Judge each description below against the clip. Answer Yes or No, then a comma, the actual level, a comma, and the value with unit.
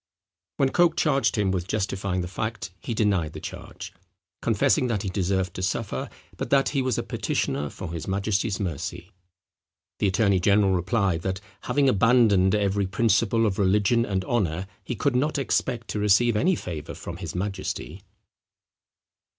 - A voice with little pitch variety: No, average, 3.7 semitones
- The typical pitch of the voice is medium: No, low, 100 Hz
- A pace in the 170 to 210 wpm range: No, average, 160 wpm